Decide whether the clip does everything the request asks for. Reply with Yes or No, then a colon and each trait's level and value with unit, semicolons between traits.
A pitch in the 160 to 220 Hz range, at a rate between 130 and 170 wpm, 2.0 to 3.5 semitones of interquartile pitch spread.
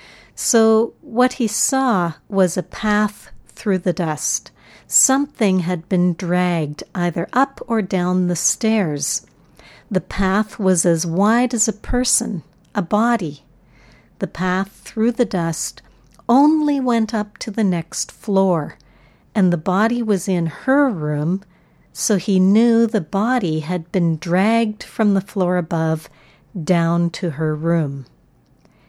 No: high, 190 Hz; slow, 135 wpm; average, 4.5 semitones